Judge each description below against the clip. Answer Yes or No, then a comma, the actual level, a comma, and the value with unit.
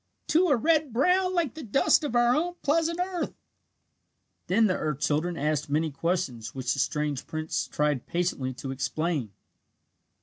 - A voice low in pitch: No, medium, 175 Hz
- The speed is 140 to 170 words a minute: Yes, average, 160 wpm